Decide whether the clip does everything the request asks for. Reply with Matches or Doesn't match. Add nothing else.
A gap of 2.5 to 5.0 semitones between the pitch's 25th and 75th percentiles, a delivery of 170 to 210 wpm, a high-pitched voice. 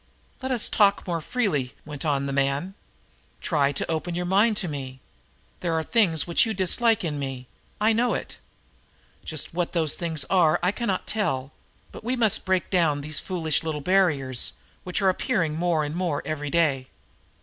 Doesn't match